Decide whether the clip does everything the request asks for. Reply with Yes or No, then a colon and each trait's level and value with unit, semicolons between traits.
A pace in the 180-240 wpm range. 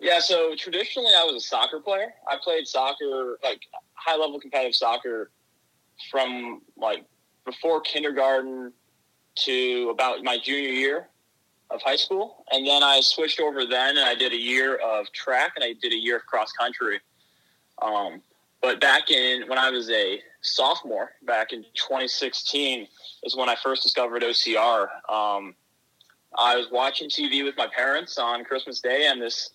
No: average, 160 wpm